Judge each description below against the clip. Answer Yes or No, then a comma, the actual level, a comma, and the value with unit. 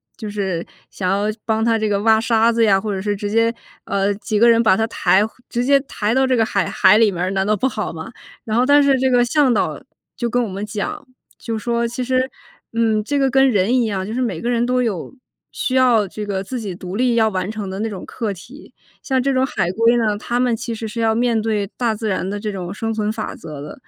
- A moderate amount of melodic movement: Yes, average, 3.0 semitones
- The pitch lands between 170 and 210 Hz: No, high, 220 Hz